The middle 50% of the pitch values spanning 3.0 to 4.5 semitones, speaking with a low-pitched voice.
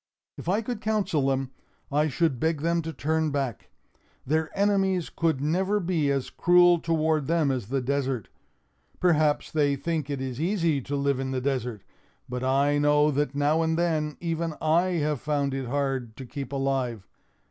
No: average, 3.4 semitones; medium, 150 Hz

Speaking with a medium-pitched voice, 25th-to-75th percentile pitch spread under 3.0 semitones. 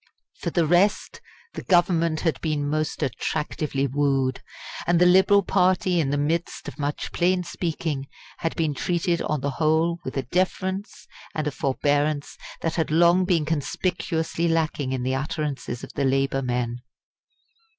No: medium, 155 Hz; average, 3.5 semitones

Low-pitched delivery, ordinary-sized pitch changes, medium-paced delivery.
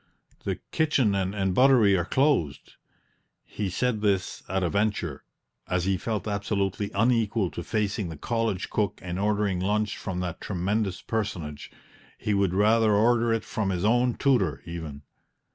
Yes: low, 100 Hz; average, 3.3 semitones; average, 150 wpm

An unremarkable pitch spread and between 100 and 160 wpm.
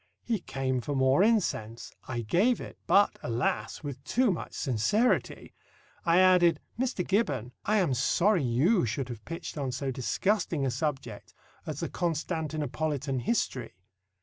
No: wide, 6.4 semitones; average, 145 wpm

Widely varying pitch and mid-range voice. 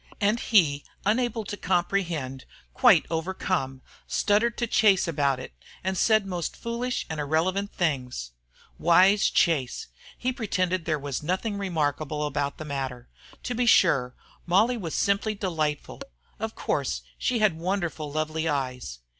Yes: wide, 5.9 semitones; medium, 175 Hz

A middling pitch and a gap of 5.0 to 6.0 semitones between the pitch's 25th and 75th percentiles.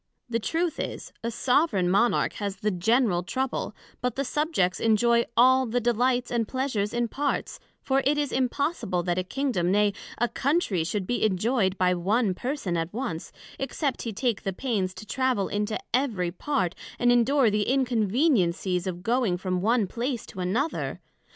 No: high, 230 Hz; wide, 5.5 semitones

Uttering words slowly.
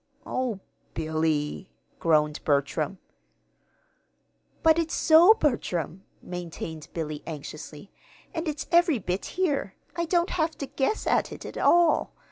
Yes: slow, 120 wpm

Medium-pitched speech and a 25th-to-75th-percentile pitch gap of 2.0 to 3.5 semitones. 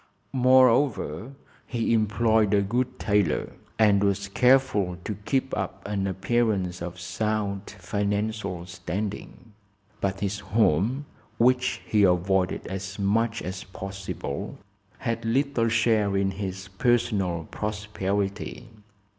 No: low, 105 Hz; average, 2.9 semitones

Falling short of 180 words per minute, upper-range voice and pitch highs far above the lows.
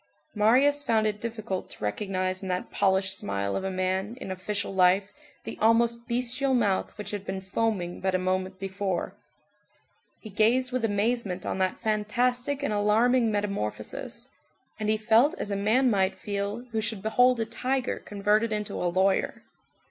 No: average, 165 wpm; high, 210 Hz; average, 3.4 semitones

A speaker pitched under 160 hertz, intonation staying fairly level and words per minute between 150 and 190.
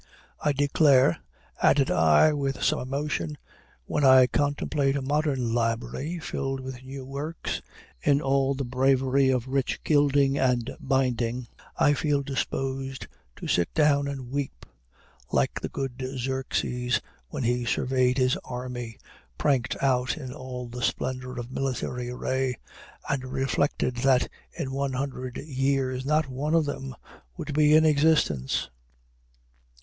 No: low, 135 Hz; narrow, 1.9 semitones; slow, 135 wpm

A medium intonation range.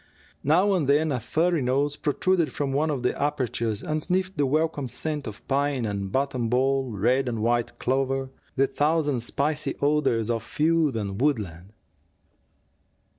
Yes: average, 3.9 semitones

